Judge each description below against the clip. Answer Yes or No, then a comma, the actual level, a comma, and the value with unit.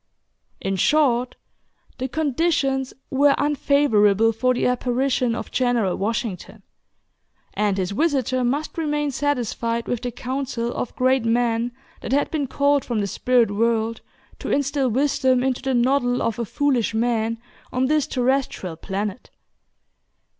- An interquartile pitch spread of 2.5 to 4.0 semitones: Yes, average, 3.3 semitones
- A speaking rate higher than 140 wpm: No, slow, 135 wpm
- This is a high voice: Yes, very high, 250 Hz